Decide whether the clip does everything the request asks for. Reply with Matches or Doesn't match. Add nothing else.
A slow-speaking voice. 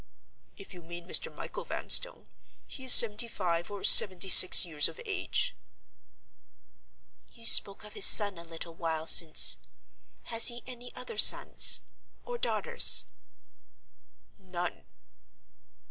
Matches